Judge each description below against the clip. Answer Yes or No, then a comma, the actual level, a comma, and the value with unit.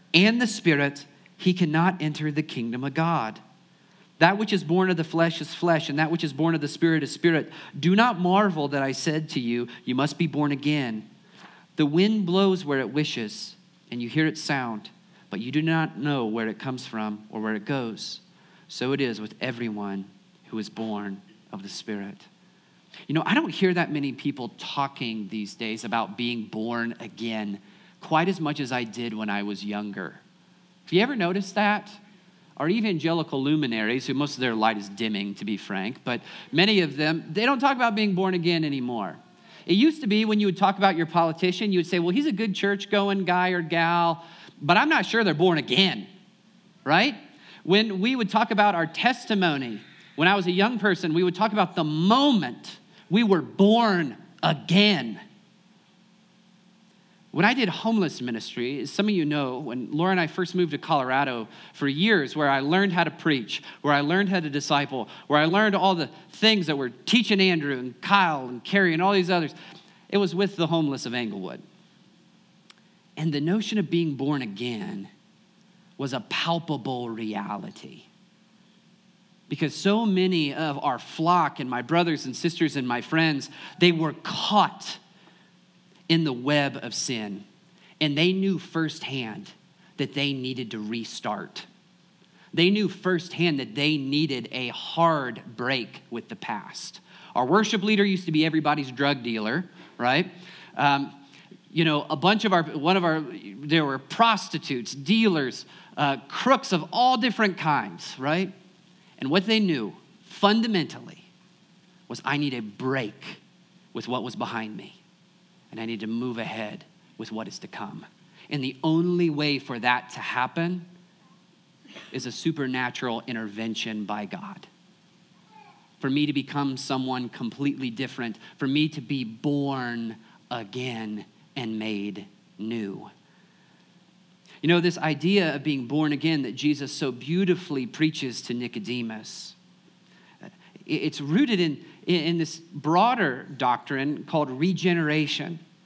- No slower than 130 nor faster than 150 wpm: No, average, 170 wpm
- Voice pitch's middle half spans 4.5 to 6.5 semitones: Yes, wide, 5.6 semitones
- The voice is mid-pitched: Yes, medium, 165 Hz